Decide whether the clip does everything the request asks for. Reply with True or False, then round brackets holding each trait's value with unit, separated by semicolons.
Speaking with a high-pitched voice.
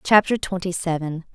False (175 Hz)